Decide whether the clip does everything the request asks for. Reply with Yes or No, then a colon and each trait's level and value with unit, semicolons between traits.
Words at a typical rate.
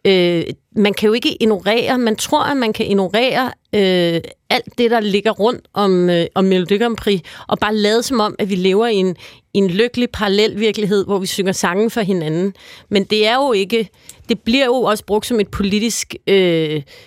Yes: average, 205 wpm